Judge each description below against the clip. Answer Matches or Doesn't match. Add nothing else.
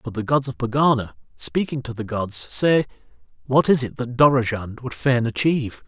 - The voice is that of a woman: Doesn't match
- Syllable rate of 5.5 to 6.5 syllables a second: Doesn't match